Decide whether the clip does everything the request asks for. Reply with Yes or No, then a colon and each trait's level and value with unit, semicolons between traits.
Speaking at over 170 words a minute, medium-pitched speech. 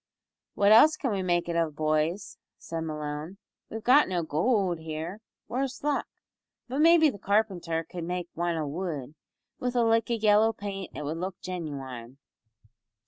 No: average, 165 wpm; medium, 180 Hz